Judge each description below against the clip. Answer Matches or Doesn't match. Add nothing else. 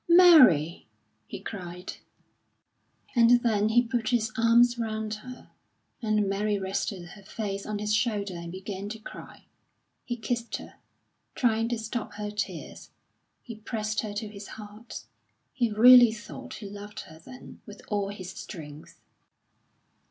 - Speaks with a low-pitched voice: Doesn't match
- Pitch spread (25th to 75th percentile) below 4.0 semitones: Matches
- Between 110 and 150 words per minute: Matches